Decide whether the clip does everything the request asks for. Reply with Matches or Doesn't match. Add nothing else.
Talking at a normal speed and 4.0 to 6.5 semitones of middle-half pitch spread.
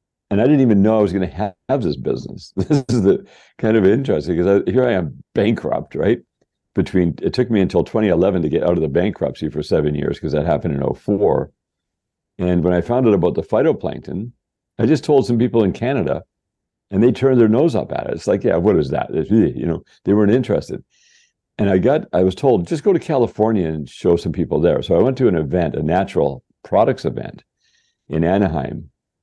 Doesn't match